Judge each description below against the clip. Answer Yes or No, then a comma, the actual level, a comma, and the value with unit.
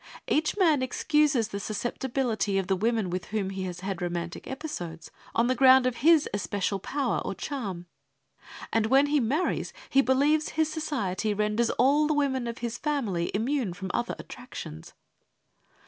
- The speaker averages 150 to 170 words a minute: Yes, average, 165 wpm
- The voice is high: Yes, high, 235 Hz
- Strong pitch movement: Yes, wide, 6.4 semitones